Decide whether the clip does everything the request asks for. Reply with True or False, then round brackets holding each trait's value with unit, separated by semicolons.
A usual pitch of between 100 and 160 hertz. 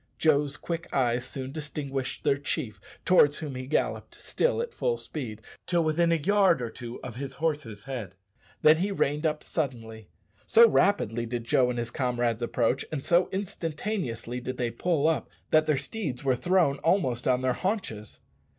True (140 Hz)